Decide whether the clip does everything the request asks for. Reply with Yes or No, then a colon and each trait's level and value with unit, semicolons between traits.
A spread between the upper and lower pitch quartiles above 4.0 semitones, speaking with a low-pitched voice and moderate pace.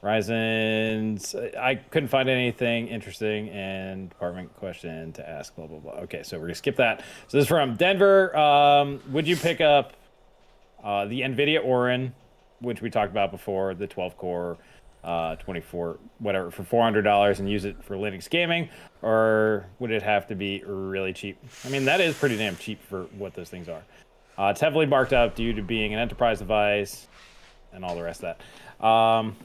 Yes: average, 4.6 semitones; low, 110 Hz; average, 190 wpm